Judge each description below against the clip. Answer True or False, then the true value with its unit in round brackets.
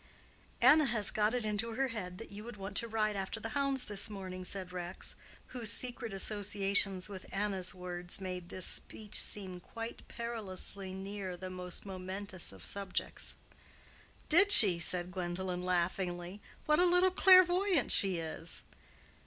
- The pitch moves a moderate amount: True (3.7 semitones)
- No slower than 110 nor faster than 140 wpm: False (155 wpm)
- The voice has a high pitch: True (195 Hz)